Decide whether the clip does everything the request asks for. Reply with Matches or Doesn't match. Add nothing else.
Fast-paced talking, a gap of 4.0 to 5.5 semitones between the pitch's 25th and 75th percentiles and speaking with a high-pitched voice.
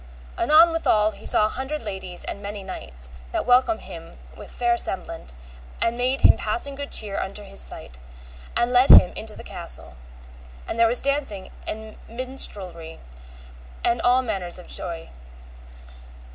Doesn't match